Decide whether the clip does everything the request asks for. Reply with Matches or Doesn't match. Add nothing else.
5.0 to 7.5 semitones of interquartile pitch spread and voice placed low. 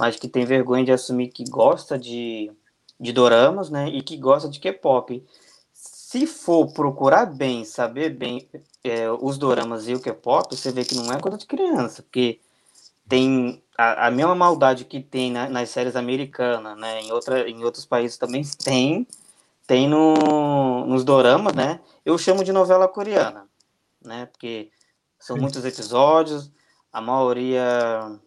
Doesn't match